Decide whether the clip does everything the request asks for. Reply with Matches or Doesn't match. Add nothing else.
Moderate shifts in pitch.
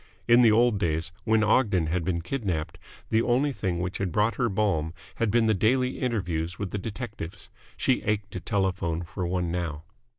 Matches